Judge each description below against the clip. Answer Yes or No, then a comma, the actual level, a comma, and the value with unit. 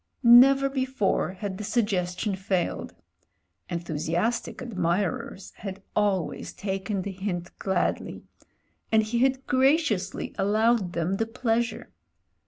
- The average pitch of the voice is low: No, high, 205 Hz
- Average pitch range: Yes, average, 4.1 semitones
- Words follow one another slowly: Yes, slow, 105 wpm